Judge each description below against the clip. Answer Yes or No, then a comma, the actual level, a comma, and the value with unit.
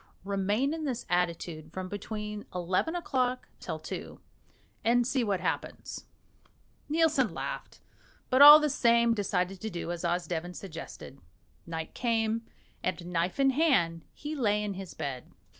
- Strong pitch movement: Yes, wide, 6.3 semitones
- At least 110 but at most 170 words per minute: Yes, average, 140 wpm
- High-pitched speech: Yes, high, 205 Hz